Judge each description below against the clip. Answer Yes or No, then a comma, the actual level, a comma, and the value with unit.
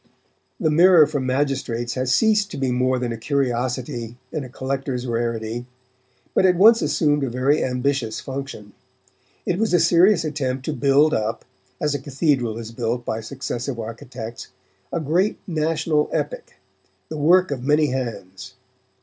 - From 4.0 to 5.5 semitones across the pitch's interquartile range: Yes, average, 4.3 semitones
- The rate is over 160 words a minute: No, average, 155 wpm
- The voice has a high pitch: No, low, 135 Hz